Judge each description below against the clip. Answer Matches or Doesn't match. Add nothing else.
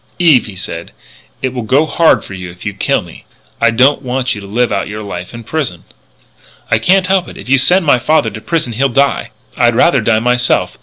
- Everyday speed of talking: Doesn't match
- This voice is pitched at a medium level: Doesn't match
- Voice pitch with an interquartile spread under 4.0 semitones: Doesn't match